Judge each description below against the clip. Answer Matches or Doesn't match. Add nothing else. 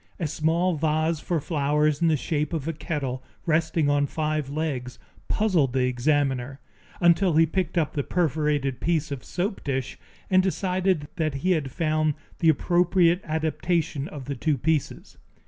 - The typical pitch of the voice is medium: Matches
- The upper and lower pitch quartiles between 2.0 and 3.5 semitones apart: Matches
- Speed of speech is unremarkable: Matches